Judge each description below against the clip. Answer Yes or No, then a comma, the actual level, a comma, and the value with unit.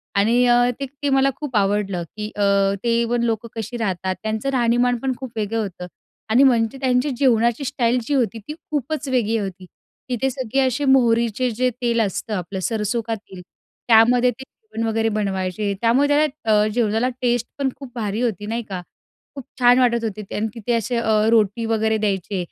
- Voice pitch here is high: Yes, high, 230 Hz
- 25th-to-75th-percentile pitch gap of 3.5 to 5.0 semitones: No, average, 3.0 semitones